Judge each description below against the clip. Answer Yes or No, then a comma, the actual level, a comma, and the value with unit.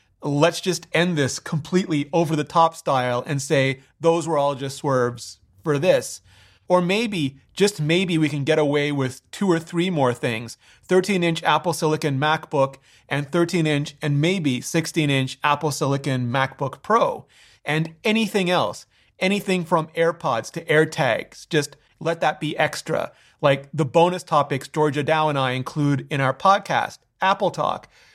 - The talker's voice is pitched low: No, medium, 155 Hz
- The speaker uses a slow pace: No, average, 160 wpm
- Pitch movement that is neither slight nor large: Yes, average, 3.7 semitones